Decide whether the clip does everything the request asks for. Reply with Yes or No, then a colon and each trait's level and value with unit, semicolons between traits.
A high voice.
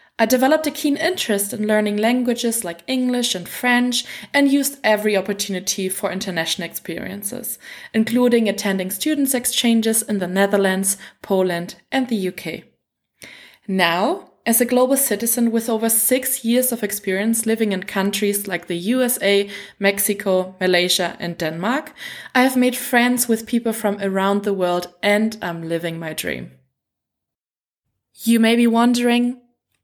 Yes: high, 215 Hz